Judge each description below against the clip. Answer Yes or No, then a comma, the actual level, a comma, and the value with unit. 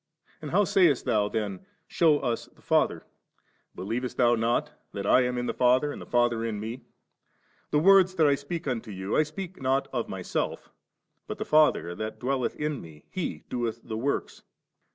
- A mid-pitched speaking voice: No, low, 125 Hz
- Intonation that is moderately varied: Yes, average, 5.0 semitones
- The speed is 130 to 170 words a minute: No, average, 180 wpm